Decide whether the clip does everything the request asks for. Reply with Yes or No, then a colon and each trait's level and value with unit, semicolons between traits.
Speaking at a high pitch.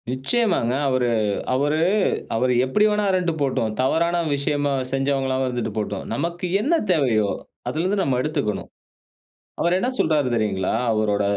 No: low, 135 Hz